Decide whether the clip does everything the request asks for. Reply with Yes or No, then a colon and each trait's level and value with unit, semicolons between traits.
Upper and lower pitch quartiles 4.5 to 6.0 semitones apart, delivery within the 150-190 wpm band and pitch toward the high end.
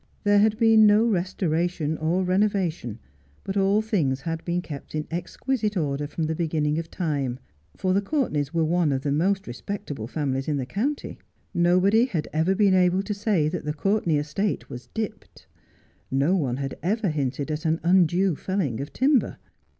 No: average, 5.0 semitones; average, 175 wpm; medium, 175 Hz